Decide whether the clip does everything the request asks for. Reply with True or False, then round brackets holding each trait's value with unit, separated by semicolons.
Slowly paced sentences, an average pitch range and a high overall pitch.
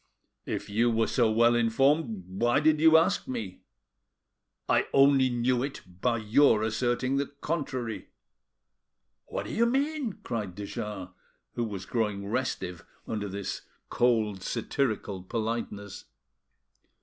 False (125 wpm; 4.3 semitones; 115 Hz)